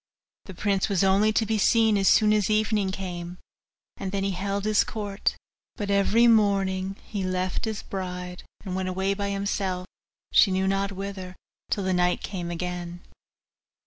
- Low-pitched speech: No, high, 195 Hz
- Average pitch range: No, narrow, 1.7 semitones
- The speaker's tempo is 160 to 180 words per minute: Yes, average, 170 wpm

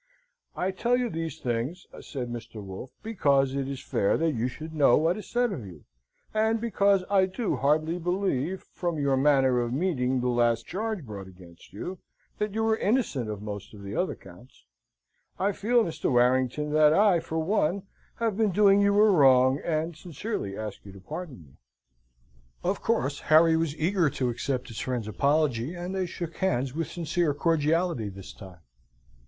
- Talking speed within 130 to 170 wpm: No, average, 180 wpm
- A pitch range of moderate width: No, wide, 7.1 semitones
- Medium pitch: Yes, medium, 155 Hz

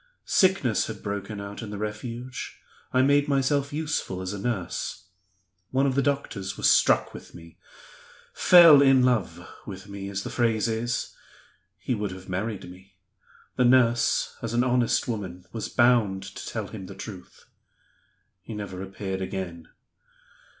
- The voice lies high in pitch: No, low, 110 Hz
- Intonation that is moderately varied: Yes, average, 4.8 semitones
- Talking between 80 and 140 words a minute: No, average, 155 wpm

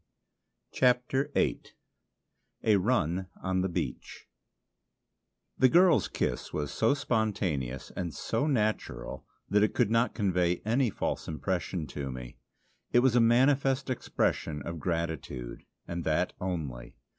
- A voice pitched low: Yes, very low, 95 Hz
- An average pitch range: No, wide, 7.2 semitones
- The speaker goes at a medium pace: No, slow, 125 wpm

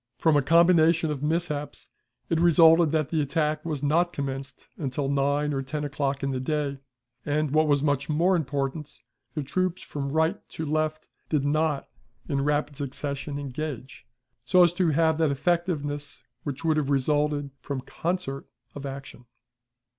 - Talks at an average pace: Yes, average, 160 wpm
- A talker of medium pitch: Yes, medium, 150 Hz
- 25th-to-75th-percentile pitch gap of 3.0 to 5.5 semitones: No, narrow, 2.4 semitones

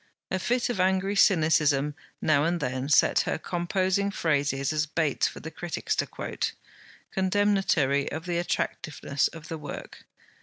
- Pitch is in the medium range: Yes, medium, 165 Hz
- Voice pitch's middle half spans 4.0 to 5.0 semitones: Yes, average, 4.4 semitones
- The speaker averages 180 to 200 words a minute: No, average, 150 wpm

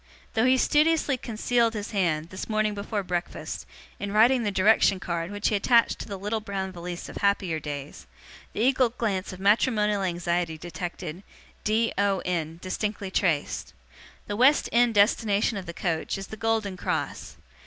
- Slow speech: No, average, 165 wpm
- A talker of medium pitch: No, high, 200 Hz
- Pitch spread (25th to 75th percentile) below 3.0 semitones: No, average, 3.8 semitones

